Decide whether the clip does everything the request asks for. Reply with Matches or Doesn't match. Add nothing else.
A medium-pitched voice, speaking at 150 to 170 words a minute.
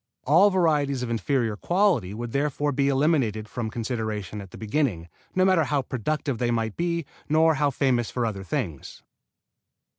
Doesn't match